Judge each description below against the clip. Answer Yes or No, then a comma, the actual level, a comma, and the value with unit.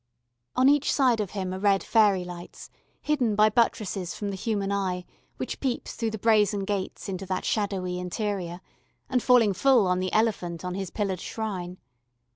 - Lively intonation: No, average, 3.1 semitones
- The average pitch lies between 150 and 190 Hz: No, high, 200 Hz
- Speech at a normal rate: Yes, average, 175 wpm